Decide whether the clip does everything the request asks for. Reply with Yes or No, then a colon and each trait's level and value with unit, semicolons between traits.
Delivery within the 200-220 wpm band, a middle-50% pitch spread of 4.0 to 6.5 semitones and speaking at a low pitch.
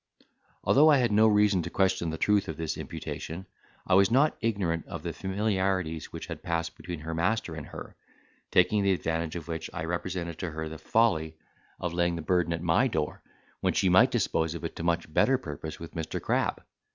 No: fast, 205 wpm; average, 3.3 semitones; very low, 85 Hz